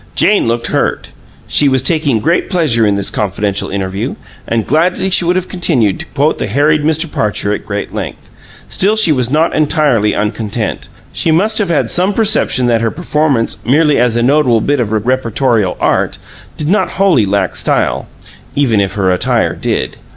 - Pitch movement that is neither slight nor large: No, wide, 6.9 semitones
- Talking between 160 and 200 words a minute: Yes, average, 175 wpm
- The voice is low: Yes, low, 130 Hz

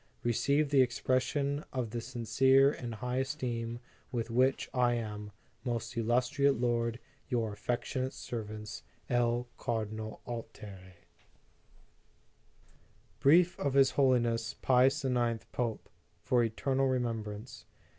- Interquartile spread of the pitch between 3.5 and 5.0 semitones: No, narrow, 2.4 semitones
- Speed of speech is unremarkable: No, slow, 110 wpm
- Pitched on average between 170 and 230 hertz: No, low, 120 Hz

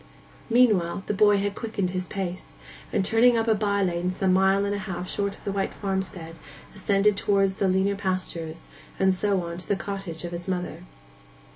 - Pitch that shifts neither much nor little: No, narrow, 1.8 semitones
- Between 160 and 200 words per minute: Yes, average, 185 wpm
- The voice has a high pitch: Yes, high, 195 Hz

